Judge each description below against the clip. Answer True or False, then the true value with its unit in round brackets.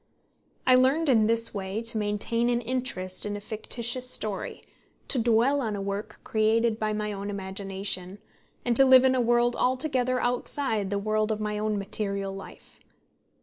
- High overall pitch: True (220 Hz)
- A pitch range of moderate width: True (3.2 semitones)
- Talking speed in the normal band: True (170 wpm)